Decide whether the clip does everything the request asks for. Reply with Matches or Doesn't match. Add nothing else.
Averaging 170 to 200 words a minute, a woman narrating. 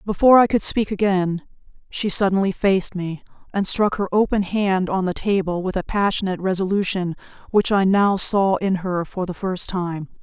Matches